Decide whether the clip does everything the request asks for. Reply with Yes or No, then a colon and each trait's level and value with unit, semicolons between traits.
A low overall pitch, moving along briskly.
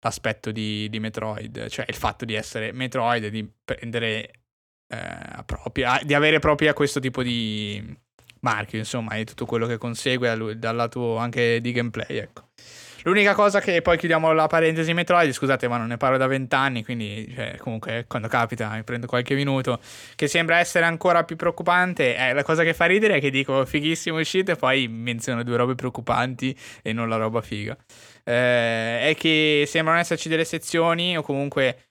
Yes: low, 125 Hz; fast, 180 wpm